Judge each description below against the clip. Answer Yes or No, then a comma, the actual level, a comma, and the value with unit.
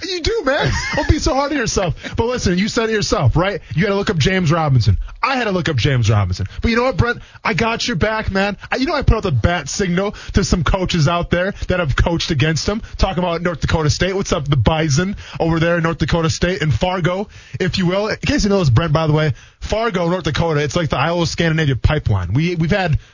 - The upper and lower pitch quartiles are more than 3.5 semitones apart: Yes, average, 4.9 semitones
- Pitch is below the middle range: No, medium, 175 Hz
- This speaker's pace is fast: Yes, fast, 260 wpm